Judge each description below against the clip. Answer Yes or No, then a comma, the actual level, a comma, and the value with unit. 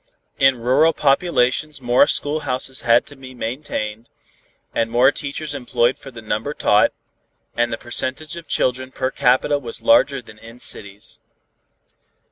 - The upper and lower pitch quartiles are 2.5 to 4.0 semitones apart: Yes, average, 3.3 semitones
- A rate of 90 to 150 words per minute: Yes, average, 140 wpm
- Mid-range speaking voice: No, low, 130 Hz